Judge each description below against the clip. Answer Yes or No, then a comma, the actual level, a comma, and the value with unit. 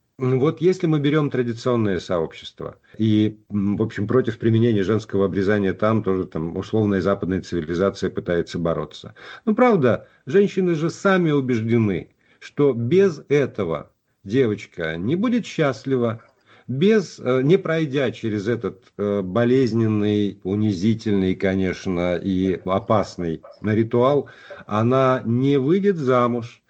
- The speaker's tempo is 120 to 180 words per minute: No, slow, 110 wpm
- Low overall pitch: Yes, low, 115 Hz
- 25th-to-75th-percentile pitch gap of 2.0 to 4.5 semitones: No, wide, 5.4 semitones